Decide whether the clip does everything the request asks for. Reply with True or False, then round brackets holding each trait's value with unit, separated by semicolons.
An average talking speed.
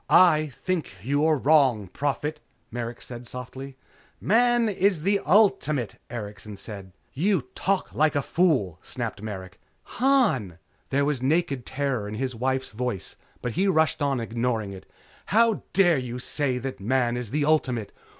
True (150 wpm)